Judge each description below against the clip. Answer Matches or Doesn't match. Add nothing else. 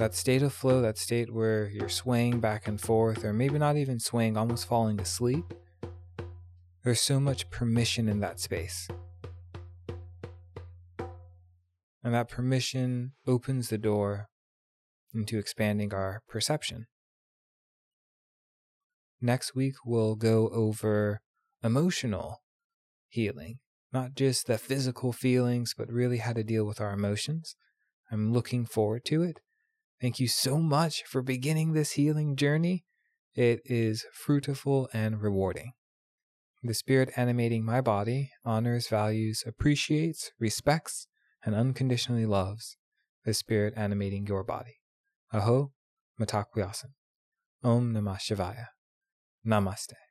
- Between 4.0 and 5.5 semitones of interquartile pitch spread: Doesn't match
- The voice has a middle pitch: Doesn't match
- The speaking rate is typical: Doesn't match